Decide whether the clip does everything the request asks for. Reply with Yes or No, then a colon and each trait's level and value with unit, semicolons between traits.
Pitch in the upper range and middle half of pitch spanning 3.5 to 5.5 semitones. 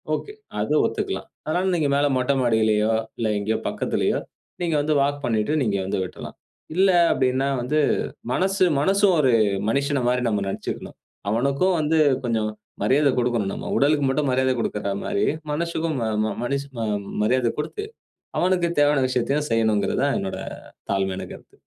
No: low, 135 Hz; average, 5.2 semitones